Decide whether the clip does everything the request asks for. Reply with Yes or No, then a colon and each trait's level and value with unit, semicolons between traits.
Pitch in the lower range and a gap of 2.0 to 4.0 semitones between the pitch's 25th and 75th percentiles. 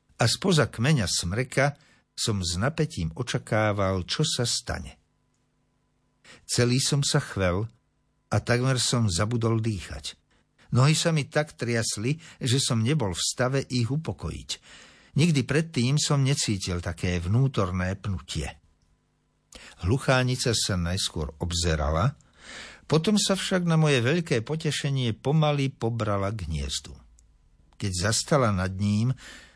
No: low, 120 Hz; wide, 7.0 semitones